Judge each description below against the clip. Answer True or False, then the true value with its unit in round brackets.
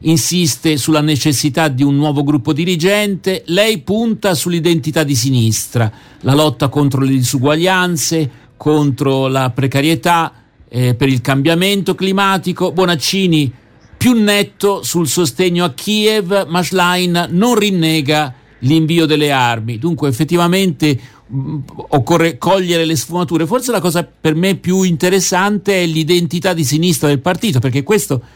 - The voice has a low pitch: False (165 Hz)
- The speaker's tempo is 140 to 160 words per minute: False (130 wpm)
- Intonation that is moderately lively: True (4.2 semitones)